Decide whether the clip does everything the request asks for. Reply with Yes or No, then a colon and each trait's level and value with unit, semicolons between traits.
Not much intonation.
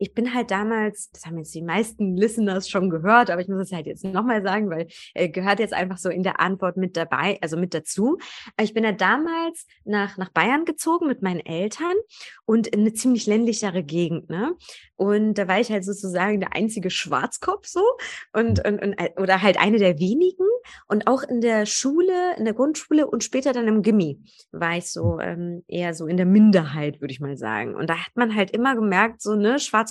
No: average, 4.2 semitones